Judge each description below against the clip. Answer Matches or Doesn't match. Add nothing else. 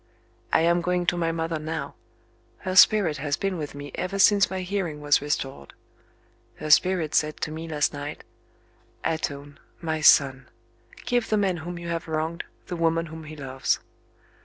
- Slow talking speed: Doesn't match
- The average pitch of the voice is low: Doesn't match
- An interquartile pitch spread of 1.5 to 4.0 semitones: Matches